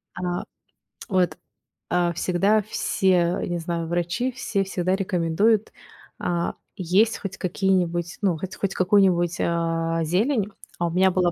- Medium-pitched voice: Yes, medium, 180 Hz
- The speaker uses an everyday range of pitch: No, narrow, 2.2 semitones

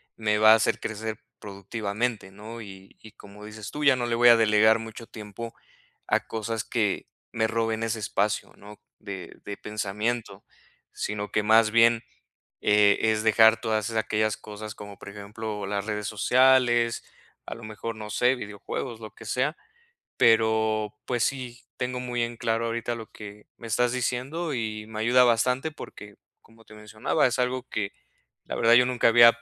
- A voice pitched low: Yes, low, 110 Hz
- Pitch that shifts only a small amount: Yes, narrow, 1.9 semitones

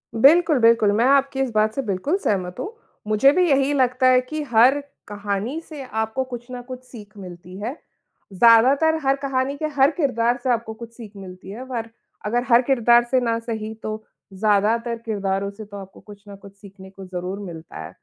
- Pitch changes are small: No, average, 4.4 semitones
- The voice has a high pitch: Yes, high, 230 Hz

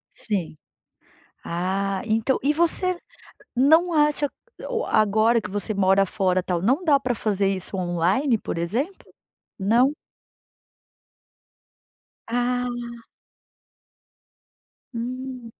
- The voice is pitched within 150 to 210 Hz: No, high, 225 Hz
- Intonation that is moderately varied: No, wide, 5.8 semitones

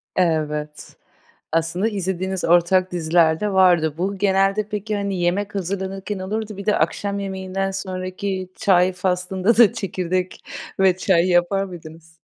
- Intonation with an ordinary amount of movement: No, narrow, 2.1 semitones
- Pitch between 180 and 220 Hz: Yes, medium, 185 Hz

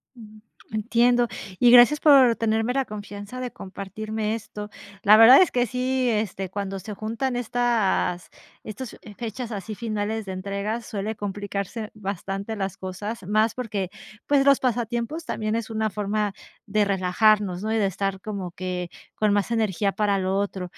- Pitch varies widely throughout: No, average, 2.8 semitones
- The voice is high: Yes, high, 215 Hz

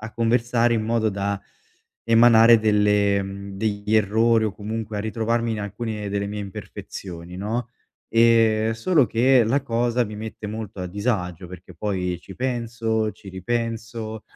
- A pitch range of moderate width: No, narrow, 2.3 semitones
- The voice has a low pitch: Yes, low, 110 Hz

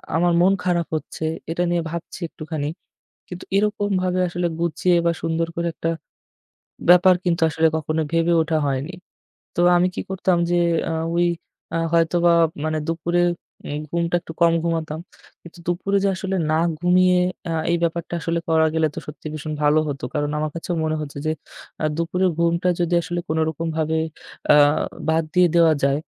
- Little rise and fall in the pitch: Yes, narrow, 1.7 semitones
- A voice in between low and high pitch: Yes, medium, 170 Hz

